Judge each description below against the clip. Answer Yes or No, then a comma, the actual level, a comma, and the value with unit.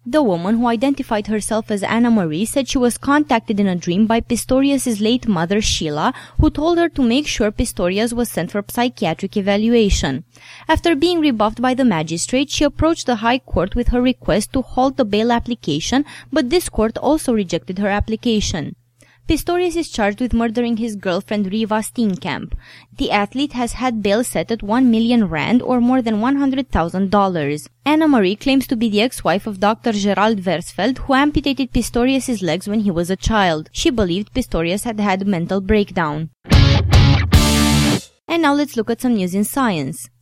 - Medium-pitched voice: No, high, 225 Hz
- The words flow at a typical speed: Yes, average, 180 wpm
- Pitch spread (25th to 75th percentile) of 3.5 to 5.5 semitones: Yes, average, 4.8 semitones